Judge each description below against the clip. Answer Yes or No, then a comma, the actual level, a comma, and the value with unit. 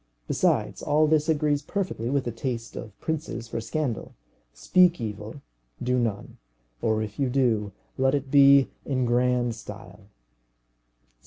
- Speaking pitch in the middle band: No, low, 125 Hz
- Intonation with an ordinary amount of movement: Yes, average, 4.2 semitones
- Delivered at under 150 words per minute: Yes, average, 140 wpm